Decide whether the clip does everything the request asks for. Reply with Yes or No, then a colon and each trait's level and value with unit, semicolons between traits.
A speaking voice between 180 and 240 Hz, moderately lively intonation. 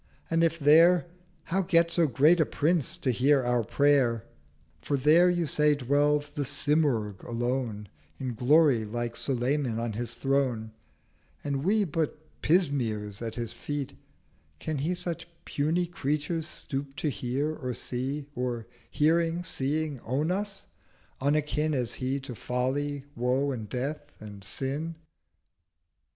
No: medium, 140 Hz; average, 4.1 semitones